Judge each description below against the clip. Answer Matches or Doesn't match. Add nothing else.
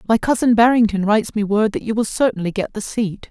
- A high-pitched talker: Matches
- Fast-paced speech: Matches